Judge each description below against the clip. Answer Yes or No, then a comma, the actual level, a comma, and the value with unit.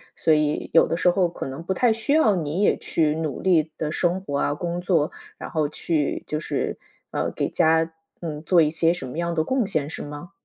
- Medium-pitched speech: Yes, medium, 165 Hz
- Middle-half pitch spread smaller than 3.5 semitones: Yes, narrow, 2.6 semitones